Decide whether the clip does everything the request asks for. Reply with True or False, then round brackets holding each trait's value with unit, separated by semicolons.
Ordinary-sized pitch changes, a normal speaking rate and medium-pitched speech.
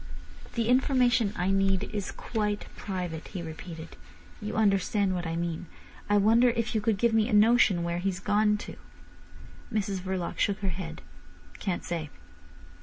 False (3.4 semitones; 160 wpm; 195 Hz)